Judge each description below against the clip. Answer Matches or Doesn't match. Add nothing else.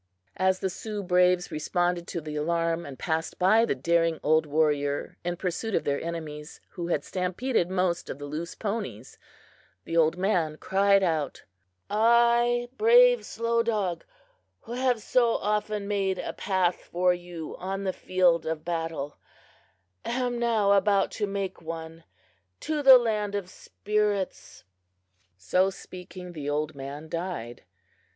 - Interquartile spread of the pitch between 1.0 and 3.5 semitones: Doesn't match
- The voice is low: Doesn't match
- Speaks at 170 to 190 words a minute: Doesn't match